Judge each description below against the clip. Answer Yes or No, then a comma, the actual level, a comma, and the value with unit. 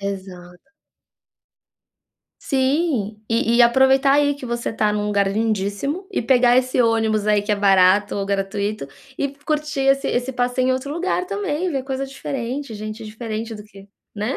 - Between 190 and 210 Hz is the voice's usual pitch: No, high, 235 Hz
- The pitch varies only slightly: No, average, 4.6 semitones